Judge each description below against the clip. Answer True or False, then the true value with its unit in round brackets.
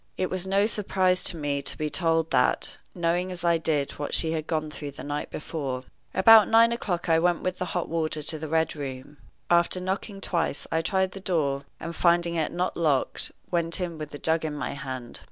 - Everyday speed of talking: False (215 wpm)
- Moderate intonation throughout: True (3.3 semitones)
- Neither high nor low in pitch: True (165 Hz)